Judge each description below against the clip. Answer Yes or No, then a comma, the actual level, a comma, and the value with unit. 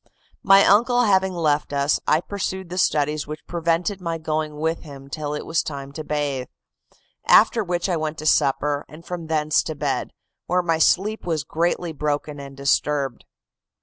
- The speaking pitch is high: No, medium, 155 Hz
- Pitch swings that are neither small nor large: Yes, average, 3.2 semitones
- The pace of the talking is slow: No, average, 175 wpm